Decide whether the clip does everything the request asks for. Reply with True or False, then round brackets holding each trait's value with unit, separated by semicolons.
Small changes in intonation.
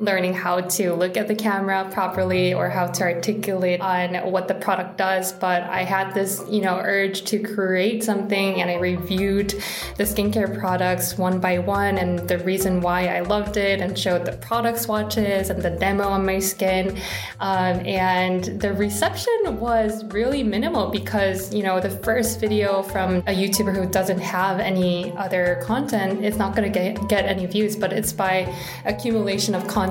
True (1.9 semitones)